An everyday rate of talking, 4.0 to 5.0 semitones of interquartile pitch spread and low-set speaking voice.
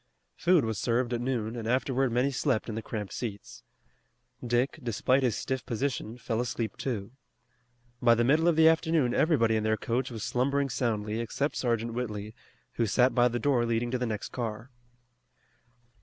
No: average, 175 wpm; average, 2.7 semitones; low, 120 Hz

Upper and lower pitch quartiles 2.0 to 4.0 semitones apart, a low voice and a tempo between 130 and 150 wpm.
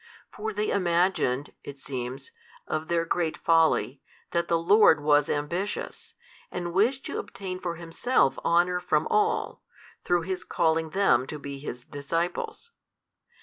No: average, 3.7 semitones; medium, 170 Hz; average, 140 wpm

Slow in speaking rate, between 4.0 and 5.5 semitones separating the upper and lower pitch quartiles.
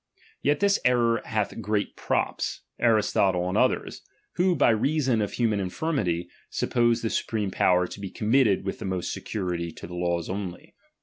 No: average, 165 wpm; average, 4.6 semitones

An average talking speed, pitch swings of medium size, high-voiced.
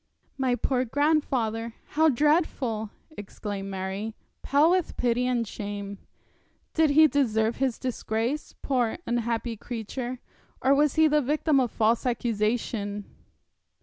No: slow, 120 wpm; average, 4.3 semitones; high, 240 Hz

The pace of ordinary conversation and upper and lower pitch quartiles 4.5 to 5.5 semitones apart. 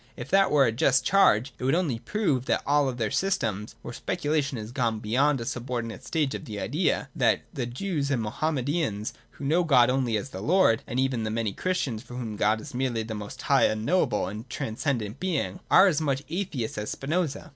No: fast, 220 wpm; average, 4.9 semitones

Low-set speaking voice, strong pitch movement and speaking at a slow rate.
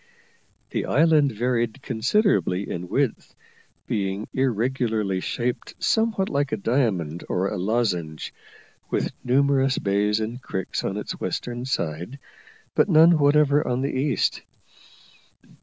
Yes: low, 120 Hz; wide, 5.9 semitones; slow, 115 wpm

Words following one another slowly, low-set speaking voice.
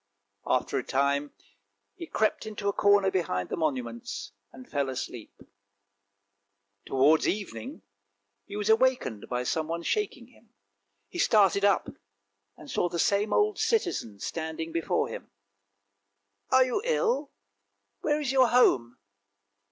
No: slow, 130 wpm; medium, 170 Hz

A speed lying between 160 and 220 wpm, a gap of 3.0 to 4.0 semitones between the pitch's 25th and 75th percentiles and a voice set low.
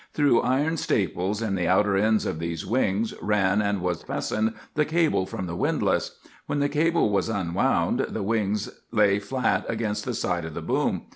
Yes: average, 185 wpm; average, 3.6 semitones; low, 105 Hz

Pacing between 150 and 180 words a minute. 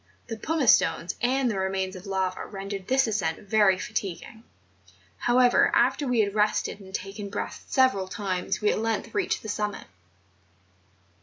Yes: average, 155 wpm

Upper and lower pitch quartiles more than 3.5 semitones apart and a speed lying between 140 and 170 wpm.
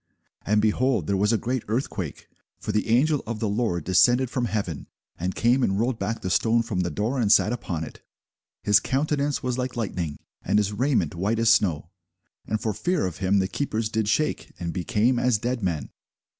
No: average, 4.3 semitones; average, 200 wpm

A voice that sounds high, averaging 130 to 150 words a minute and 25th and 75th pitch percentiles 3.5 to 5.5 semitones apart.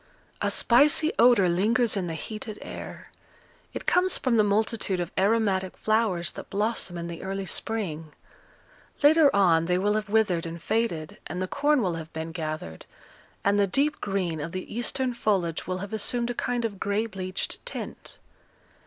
No: high, 200 Hz; average, 170 wpm; average, 4.6 semitones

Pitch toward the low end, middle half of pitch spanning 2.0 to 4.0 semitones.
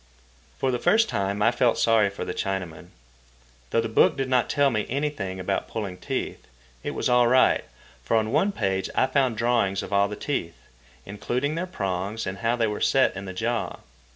No: low, 115 Hz; average, 4.7 semitones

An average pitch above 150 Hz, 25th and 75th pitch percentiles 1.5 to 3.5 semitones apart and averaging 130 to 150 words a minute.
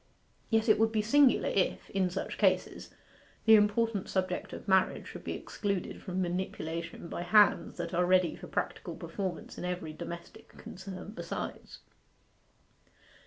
Yes: high, 190 Hz; average, 2.9 semitones; average, 145 wpm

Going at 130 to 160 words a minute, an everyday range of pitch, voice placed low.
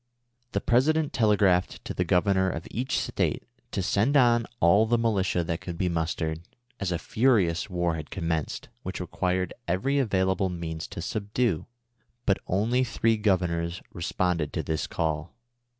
Yes: average, 155 wpm; average, 4.7 semitones; very low, 95 Hz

